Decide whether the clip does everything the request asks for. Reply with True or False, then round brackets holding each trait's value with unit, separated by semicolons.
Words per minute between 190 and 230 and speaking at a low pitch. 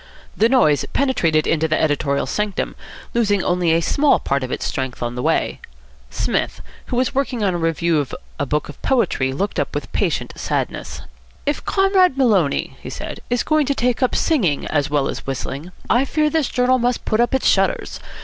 False (195 wpm; 200 Hz)